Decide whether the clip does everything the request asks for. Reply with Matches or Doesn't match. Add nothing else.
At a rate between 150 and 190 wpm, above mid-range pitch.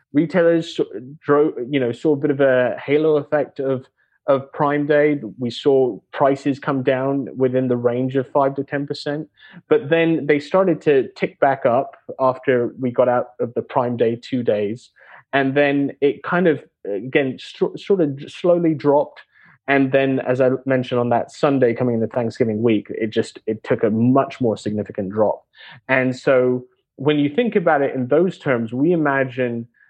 Doesn't match